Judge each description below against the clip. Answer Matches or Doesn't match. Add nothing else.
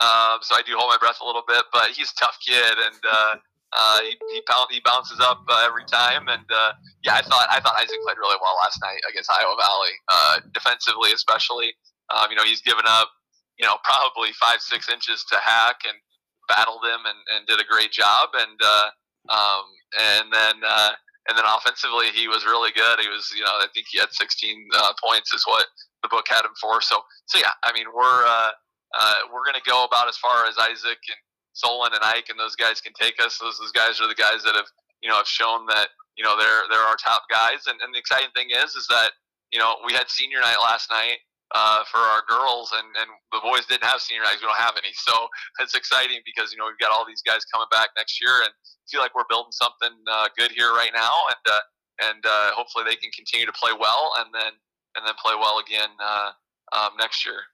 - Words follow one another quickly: Matches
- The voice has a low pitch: Doesn't match